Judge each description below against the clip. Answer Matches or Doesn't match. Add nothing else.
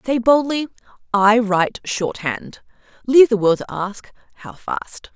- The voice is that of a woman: Matches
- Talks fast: Doesn't match